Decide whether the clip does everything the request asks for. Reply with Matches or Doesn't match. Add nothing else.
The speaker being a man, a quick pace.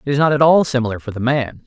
Matches